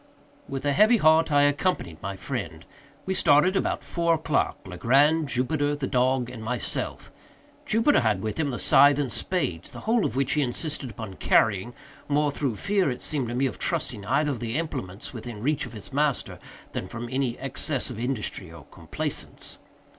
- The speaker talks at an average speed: Yes, average, 175 wpm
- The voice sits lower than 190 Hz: Yes, low, 135 Hz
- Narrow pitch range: No, average, 4.5 semitones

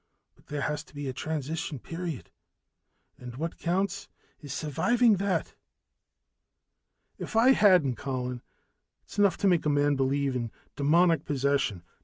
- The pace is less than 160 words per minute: Yes, average, 140 wpm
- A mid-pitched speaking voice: Yes, medium, 150 Hz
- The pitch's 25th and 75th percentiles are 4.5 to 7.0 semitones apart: Yes, average, 4.8 semitones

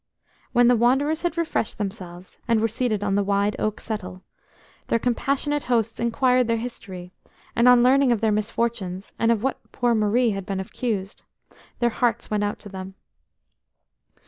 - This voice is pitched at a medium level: No, high, 225 Hz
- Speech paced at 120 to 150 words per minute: No, average, 170 wpm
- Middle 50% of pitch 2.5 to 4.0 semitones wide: Yes, average, 3.4 semitones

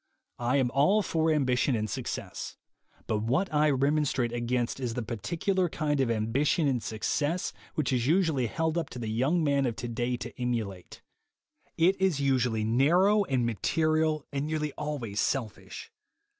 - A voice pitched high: No, low, 135 Hz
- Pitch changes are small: No, average, 4.7 semitones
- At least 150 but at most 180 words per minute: Yes, average, 160 wpm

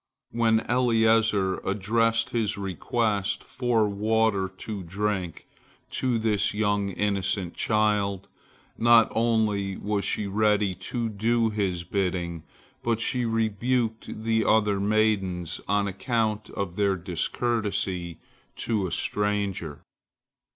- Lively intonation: No, narrow, 2.5 semitones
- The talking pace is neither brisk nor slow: No, slow, 110 wpm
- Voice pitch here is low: Yes, low, 105 Hz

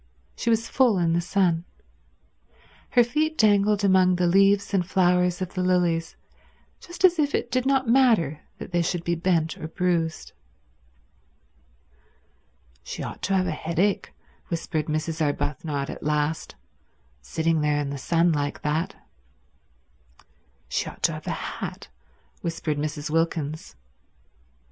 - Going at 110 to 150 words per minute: Yes, average, 140 wpm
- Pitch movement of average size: Yes, average, 4.0 semitones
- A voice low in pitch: No, medium, 175 Hz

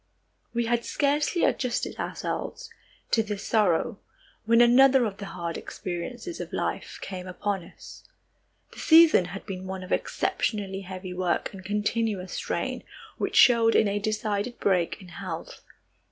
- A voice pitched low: No, high, 205 Hz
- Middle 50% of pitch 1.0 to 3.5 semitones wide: No, average, 4.2 semitones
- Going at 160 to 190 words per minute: No, average, 145 wpm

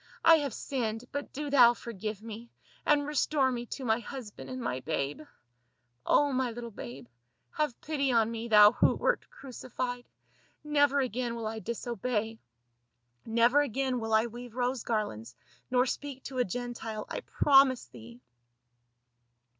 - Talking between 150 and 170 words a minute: Yes, average, 155 wpm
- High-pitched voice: Yes, high, 240 Hz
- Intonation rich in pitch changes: No, average, 3.2 semitones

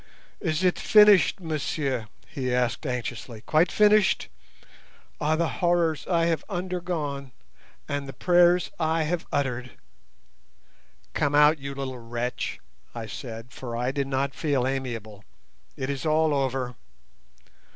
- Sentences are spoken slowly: Yes, slow, 130 wpm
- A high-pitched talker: No, medium, 140 Hz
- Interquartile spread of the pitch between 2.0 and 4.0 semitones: No, average, 4.7 semitones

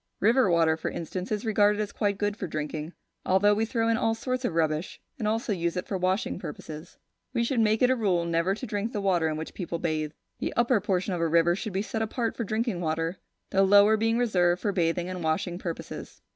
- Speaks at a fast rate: Yes, fast, 235 wpm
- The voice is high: Yes, high, 195 Hz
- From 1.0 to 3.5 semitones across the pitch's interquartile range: No, average, 4.4 semitones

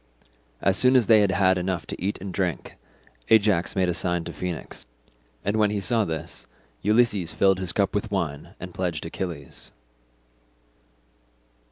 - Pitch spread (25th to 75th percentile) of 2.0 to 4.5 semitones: Yes, average, 2.9 semitones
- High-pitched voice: No, very low, 95 Hz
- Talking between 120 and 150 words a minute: No, average, 160 wpm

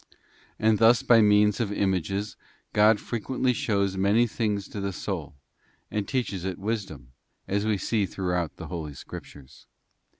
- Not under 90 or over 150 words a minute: Yes, average, 145 wpm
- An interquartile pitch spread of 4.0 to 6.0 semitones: No, narrow, 2.4 semitones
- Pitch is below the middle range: Yes, low, 100 Hz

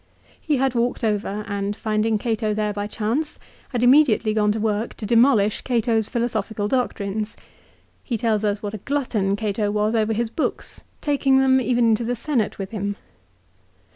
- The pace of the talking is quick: No, average, 170 wpm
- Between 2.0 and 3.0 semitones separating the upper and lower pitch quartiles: Yes, narrow, 2.6 semitones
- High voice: Yes, high, 220 Hz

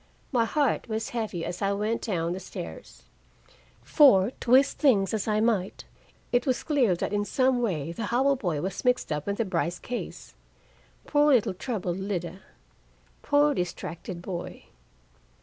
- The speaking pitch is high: Yes, high, 210 Hz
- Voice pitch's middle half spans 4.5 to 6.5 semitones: Yes, wide, 5.5 semitones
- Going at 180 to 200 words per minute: No, average, 155 wpm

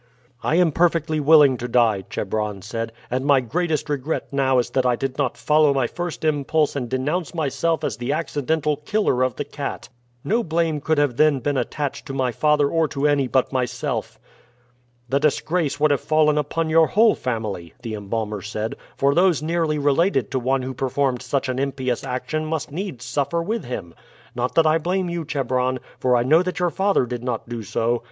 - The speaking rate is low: No, average, 195 wpm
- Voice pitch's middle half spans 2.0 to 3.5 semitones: No, average, 3.9 semitones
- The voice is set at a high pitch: No, medium, 140 Hz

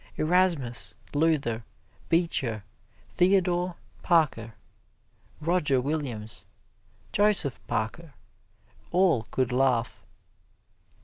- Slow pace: Yes, slow, 65 wpm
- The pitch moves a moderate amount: No, wide, 6.7 semitones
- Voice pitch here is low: No, medium, 150 Hz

